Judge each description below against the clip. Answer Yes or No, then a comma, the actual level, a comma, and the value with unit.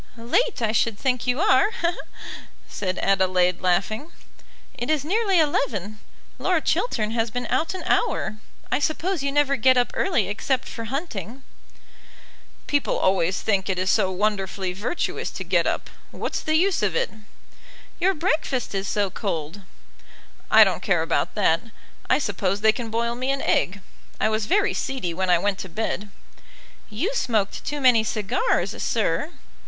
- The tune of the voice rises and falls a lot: Yes, wide, 6.5 semitones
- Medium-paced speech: Yes, average, 160 wpm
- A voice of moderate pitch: No, high, 225 Hz